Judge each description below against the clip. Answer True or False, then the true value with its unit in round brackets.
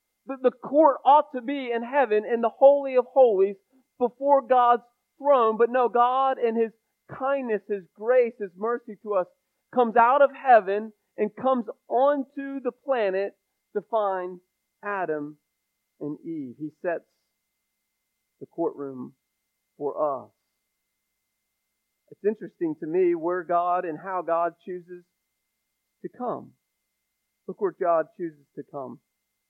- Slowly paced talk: True (130 wpm)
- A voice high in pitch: True (235 Hz)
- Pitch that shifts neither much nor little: False (6.0 semitones)